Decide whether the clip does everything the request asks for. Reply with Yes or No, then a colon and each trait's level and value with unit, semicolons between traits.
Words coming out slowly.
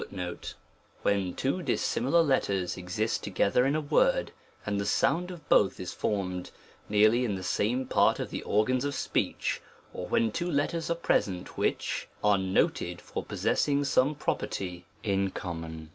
No: average, 160 wpm